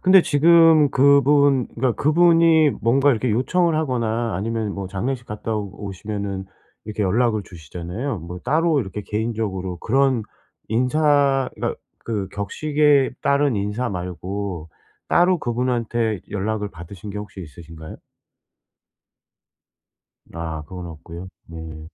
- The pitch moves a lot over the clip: Yes, wide, 6.5 semitones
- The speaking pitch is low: Yes, low, 110 Hz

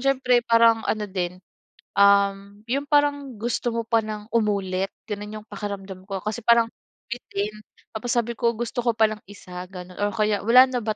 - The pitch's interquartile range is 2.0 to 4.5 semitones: Yes, average, 2.9 semitones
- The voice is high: Yes, high, 215 Hz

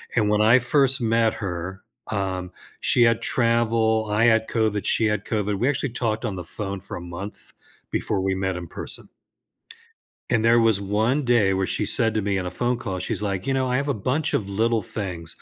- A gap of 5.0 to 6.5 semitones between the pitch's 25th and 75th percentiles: No, average, 3.3 semitones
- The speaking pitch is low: Yes, low, 110 Hz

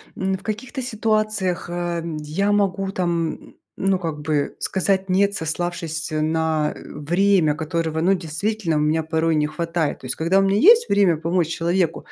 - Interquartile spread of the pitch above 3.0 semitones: Yes, average, 3.4 semitones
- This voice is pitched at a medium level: Yes, medium, 175 Hz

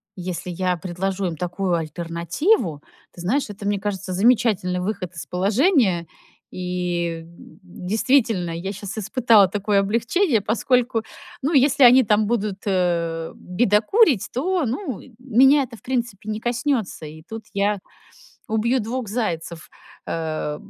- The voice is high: Yes, high, 205 Hz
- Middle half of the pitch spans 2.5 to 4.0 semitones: No, average, 5.1 semitones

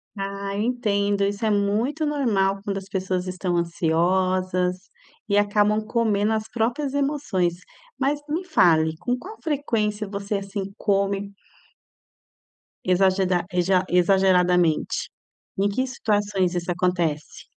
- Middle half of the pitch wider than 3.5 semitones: No, average, 3.0 semitones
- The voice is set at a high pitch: Yes, high, 200 Hz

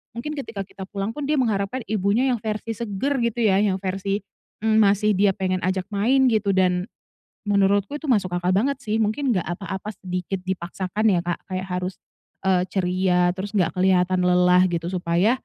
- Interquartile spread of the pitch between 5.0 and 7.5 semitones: No, average, 2.9 semitones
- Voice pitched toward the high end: Yes, high, 195 Hz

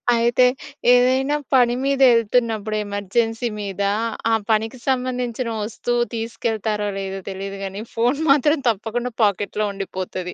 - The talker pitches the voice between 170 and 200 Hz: No, high, 230 Hz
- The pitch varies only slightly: No, average, 3.5 semitones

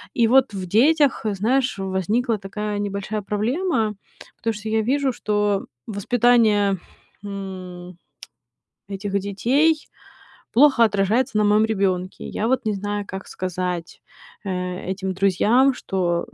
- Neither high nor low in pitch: No, high, 205 Hz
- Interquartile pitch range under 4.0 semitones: Yes, average, 3.4 semitones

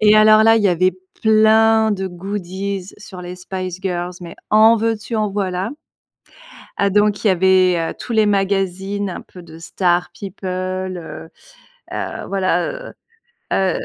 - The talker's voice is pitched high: Yes, high, 195 Hz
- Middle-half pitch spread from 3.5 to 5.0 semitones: No, narrow, 2.6 semitones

